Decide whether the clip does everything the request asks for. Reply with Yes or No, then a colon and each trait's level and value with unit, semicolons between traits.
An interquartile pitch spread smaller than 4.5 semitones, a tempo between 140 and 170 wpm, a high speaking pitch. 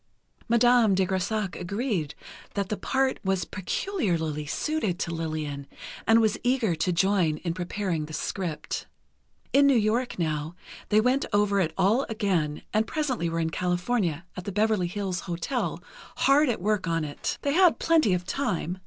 No: average, 5.3 semitones; average, 160 wpm; high, 195 Hz